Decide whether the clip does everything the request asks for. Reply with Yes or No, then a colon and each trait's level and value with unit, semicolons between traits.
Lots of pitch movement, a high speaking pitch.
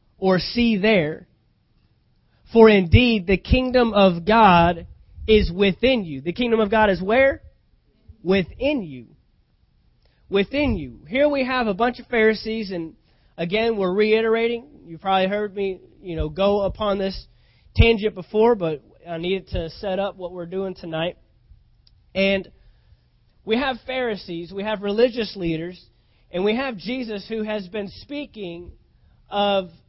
No: average, 3.9 semitones; high, 200 Hz